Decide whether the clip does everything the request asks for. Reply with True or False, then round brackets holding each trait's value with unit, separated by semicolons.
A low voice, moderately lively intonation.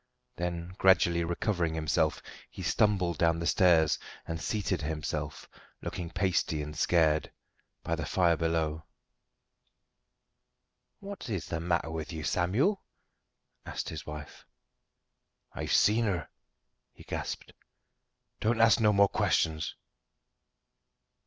True (85 Hz; 3.3 semitones)